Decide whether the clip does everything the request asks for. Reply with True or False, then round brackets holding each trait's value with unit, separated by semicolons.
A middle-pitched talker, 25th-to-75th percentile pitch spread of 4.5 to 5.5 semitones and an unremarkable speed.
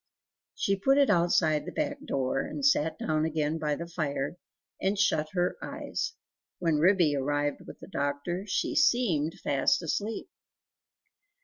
True (165 Hz; 5.0 semitones; 145 wpm)